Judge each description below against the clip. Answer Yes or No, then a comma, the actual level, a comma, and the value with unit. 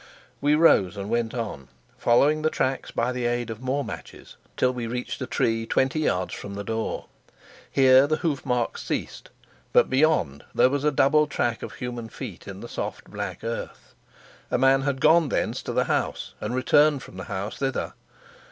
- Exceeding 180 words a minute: Yes, average, 190 wpm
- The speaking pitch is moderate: No, low, 125 Hz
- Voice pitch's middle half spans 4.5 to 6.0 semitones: No, average, 3.8 semitones